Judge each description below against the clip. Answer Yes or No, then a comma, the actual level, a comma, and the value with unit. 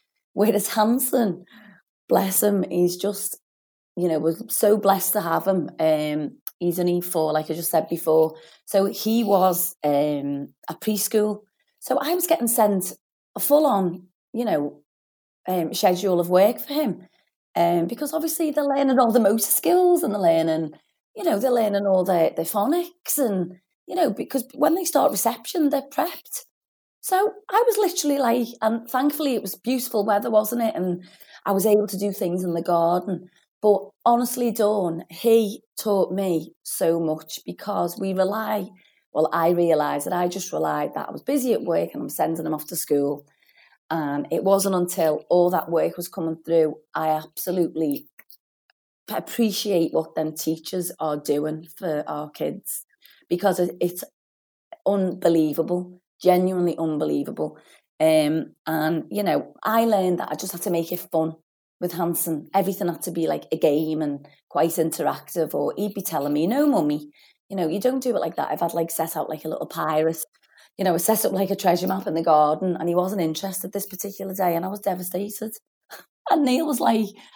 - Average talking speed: Yes, average, 180 wpm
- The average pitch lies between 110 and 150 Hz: No, medium, 185 Hz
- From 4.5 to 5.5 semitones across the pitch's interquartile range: Yes, average, 5.1 semitones